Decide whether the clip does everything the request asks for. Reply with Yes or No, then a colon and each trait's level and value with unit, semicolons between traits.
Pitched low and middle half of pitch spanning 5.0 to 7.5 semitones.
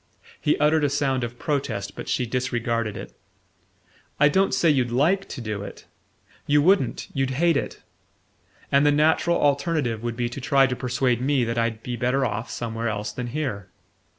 No: low, 130 Hz; average, 3.8 semitones